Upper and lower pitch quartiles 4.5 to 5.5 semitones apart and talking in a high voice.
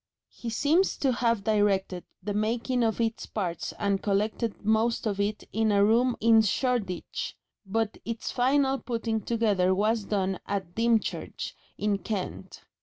No: narrow, 2.5 semitones; high, 220 Hz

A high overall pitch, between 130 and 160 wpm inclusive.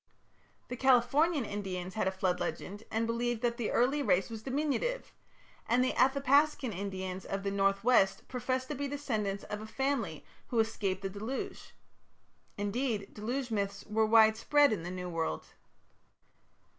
Yes: high, 220 Hz; average, 155 wpm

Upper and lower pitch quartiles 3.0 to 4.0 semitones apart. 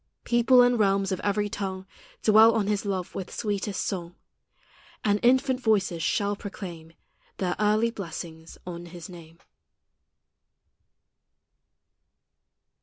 Yes: average, 3.4 semitones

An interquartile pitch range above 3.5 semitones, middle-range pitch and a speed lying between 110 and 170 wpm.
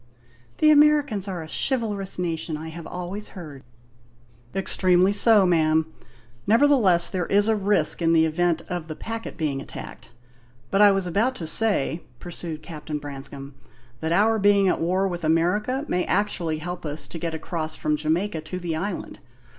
Yes: average, 4.2 semitones; medium, 175 Hz; average, 165 wpm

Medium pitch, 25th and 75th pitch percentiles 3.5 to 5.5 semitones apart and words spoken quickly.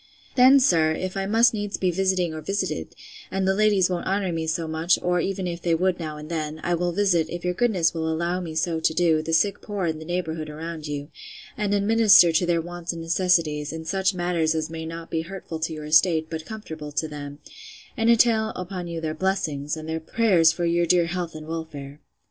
No: medium, 170 Hz; average, 2.9 semitones; fast, 225 wpm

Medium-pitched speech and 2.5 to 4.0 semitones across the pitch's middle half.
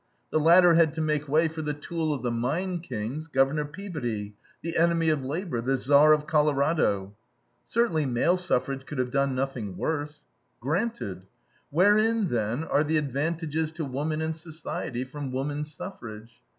Yes: medium, 150 Hz; average, 3.7 semitones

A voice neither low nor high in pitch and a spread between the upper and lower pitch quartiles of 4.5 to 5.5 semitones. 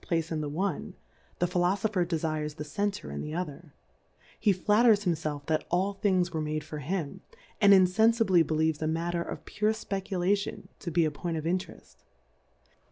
No: medium, 175 Hz; average, 4.0 semitones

